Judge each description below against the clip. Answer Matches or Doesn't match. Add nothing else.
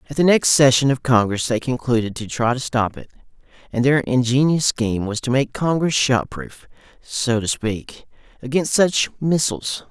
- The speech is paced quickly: Doesn't match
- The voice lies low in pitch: Matches